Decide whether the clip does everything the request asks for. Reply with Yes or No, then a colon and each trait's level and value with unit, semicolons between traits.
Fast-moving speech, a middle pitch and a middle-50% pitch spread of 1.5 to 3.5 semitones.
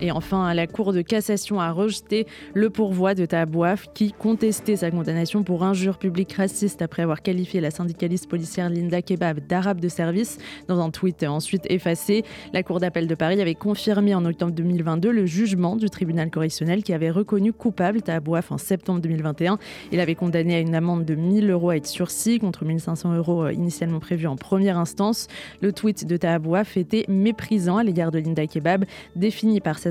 Yes: fast, 190 wpm; medium, 180 Hz; average, 3.2 semitones